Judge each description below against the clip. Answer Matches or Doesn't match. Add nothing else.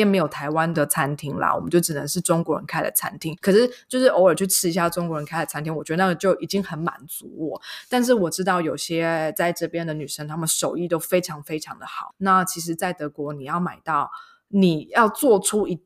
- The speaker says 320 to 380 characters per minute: Matches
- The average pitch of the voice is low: Doesn't match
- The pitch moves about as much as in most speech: Matches